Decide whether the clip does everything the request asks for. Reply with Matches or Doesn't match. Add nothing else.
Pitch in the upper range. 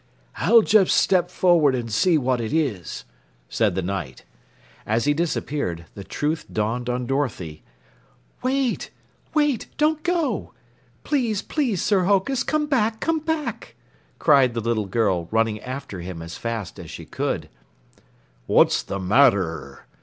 Doesn't match